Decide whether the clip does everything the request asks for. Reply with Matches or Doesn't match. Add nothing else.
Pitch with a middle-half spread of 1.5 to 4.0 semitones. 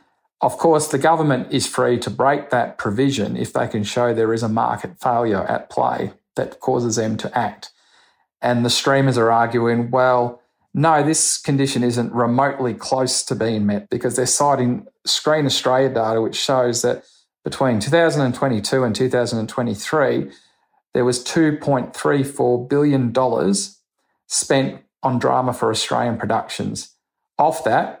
Matches